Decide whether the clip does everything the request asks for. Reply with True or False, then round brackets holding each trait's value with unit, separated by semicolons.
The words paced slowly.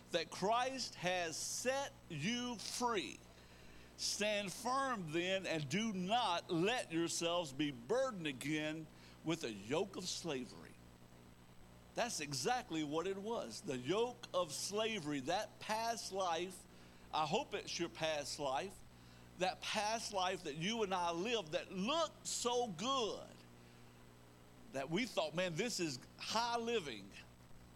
True (130 wpm)